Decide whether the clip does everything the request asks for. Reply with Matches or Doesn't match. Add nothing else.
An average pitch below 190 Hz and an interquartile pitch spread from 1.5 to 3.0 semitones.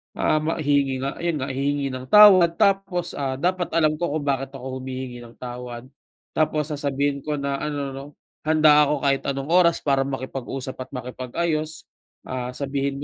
Matches